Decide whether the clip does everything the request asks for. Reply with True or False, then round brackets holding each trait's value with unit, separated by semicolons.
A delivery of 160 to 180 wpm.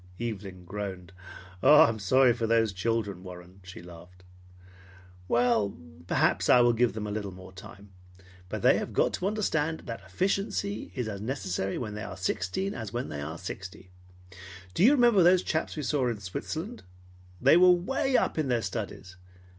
True (170 wpm)